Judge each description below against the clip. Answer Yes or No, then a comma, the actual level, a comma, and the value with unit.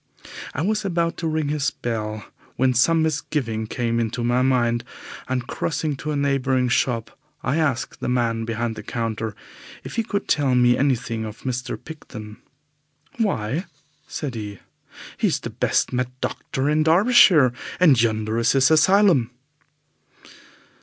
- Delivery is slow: No, average, 150 wpm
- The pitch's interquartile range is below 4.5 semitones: No, average, 4.9 semitones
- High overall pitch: No, low, 130 Hz